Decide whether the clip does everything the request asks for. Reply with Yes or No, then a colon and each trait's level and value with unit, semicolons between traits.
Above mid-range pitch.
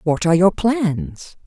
No: medium, 170 Hz